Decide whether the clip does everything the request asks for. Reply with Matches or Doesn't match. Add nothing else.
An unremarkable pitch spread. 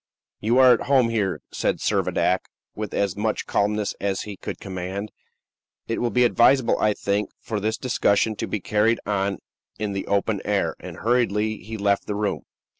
Doesn't match